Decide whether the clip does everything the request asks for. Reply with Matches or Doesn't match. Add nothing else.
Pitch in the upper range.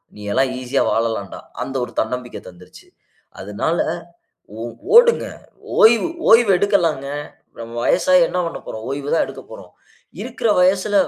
Doesn't match